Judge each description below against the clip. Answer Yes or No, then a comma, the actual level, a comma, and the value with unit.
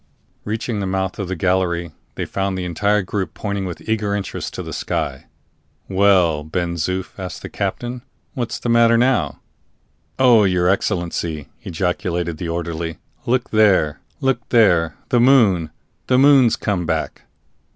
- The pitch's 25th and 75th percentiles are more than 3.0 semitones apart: Yes, average, 4.5 semitones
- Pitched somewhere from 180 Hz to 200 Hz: No, very low, 95 Hz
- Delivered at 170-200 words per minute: No, average, 150 wpm